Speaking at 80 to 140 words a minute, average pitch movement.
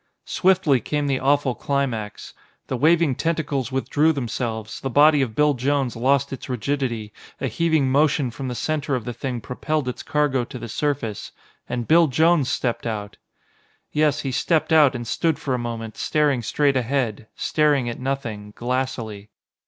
No: average, 165 wpm; average, 3.7 semitones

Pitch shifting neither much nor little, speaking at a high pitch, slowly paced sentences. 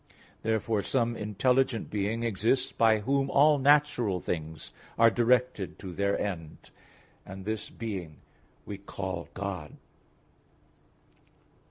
No: average, 4.3 semitones; low, 110 Hz; slow, 110 wpm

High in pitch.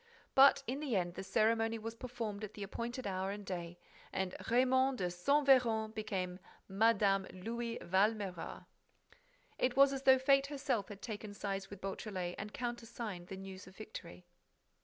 Yes: high, 215 Hz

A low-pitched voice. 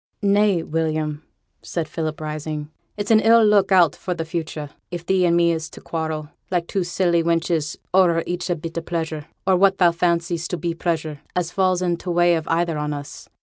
No: medium, 170 Hz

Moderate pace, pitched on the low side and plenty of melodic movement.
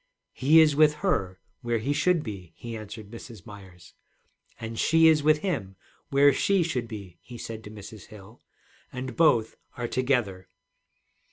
Yes: average, 160 wpm; low, 120 Hz; wide, 6.2 semitones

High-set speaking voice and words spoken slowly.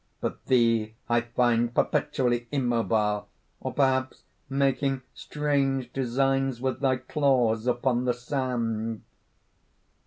No: low, 125 Hz; slow, 100 wpm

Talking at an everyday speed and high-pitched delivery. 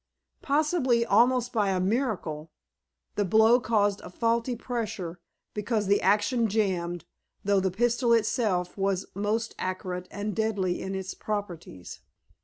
No: slow, 130 wpm; high, 205 Hz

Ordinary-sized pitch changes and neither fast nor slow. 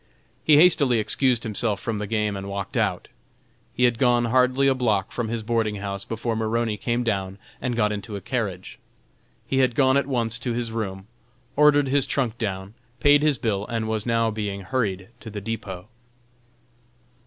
Yes: average, 3.4 semitones; average, 180 wpm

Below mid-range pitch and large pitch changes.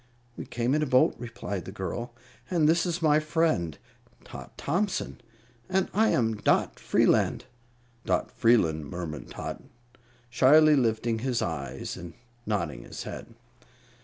Yes: low, 120 Hz; wide, 8.4 semitones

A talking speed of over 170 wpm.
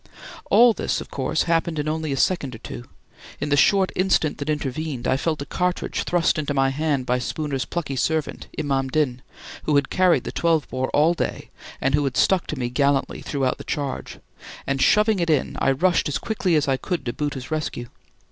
Yes: fast, 205 wpm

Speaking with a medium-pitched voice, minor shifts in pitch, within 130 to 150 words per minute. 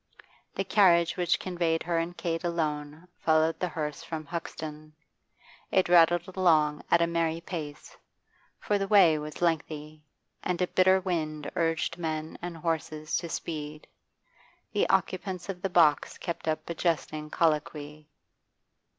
Yes: medium, 165 Hz; narrow, 2.2 semitones; average, 140 wpm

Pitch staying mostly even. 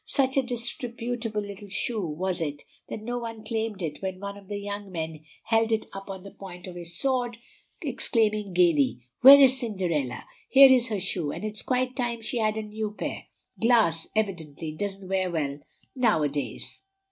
No: average, 4.7 semitones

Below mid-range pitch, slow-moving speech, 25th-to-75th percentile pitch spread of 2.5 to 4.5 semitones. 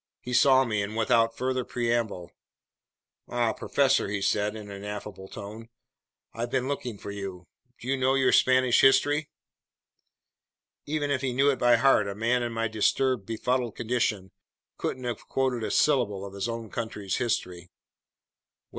No: low, 115 Hz; average, 165 wpm; average, 3.9 semitones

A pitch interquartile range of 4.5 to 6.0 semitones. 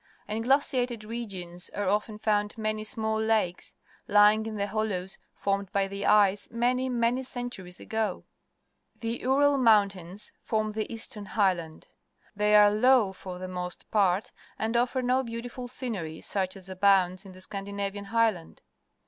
No: average, 3.0 semitones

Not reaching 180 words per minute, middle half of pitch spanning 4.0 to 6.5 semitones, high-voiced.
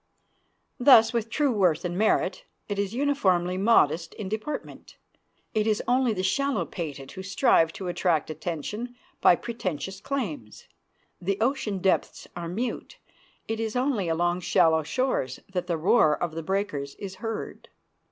Yes: average, 150 wpm; average, 5.1 semitones; high, 195 Hz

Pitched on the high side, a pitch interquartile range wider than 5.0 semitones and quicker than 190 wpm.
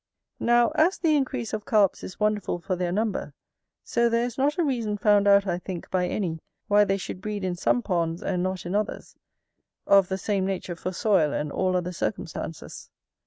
No: high, 195 Hz; average, 3.2 semitones; average, 200 wpm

